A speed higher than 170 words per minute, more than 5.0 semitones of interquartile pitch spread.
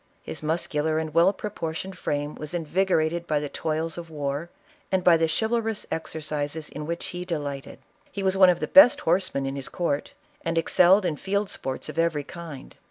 No: average, 185 wpm; average, 3.2 semitones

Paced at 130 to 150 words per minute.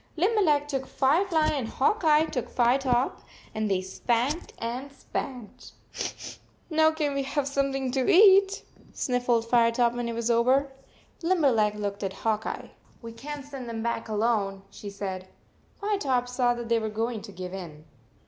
No: average, 170 wpm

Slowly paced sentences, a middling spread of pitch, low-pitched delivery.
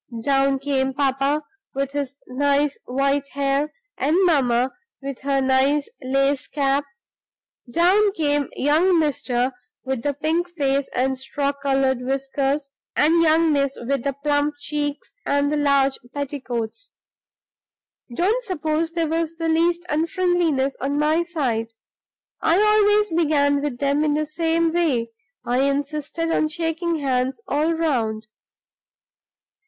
No: slow, 130 wpm; average, 3.1 semitones; very high, 285 Hz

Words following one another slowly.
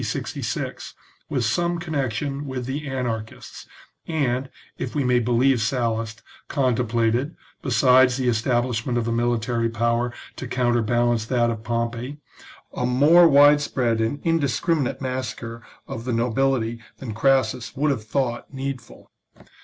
Yes: slow, 130 wpm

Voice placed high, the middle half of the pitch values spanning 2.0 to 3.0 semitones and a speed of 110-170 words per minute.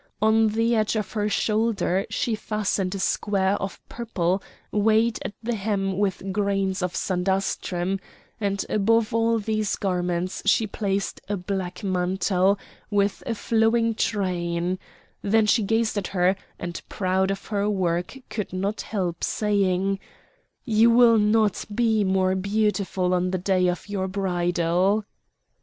Yes: high, 200 Hz; narrow, 2.6 semitones; average, 140 wpm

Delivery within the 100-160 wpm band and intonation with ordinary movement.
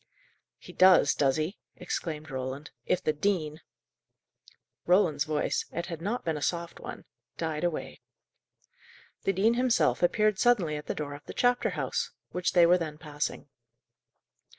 Yes: average, 155 wpm; average, 3.7 semitones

